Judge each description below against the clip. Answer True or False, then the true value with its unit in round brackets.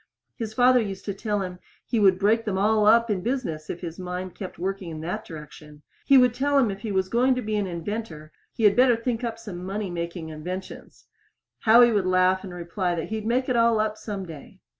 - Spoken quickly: True (230 wpm)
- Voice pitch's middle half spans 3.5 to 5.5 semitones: True (4.1 semitones)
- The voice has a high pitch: True (200 Hz)